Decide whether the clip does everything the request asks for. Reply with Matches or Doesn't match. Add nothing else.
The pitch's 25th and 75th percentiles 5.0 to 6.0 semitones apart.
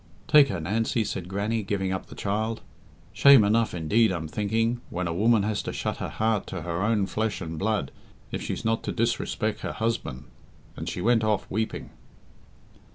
Doesn't match